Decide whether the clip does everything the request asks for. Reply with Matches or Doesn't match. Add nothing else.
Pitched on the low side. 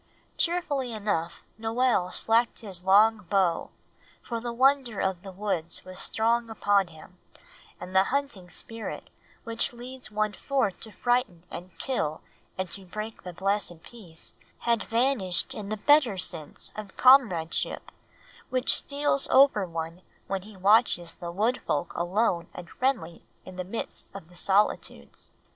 Doesn't match